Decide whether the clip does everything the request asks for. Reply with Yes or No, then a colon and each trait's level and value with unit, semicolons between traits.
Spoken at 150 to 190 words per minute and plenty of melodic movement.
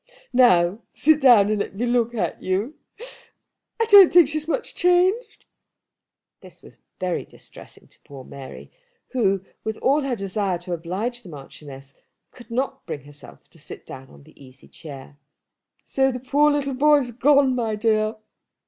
Yes: average, 165 wpm; wide, 7.8 semitones